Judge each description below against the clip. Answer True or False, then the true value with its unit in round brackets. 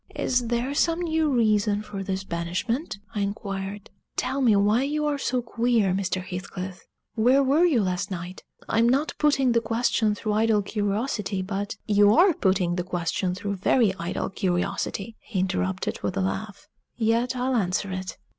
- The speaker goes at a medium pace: True (170 wpm)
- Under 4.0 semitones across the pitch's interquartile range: False (4.4 semitones)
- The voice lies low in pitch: False (210 Hz)